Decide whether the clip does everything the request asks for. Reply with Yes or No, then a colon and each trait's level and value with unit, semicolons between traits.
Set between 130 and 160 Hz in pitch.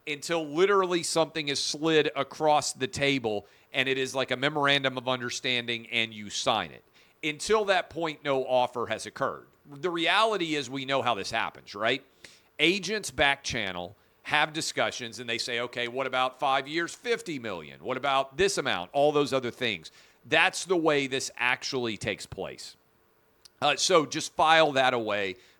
Yes: low, 135 Hz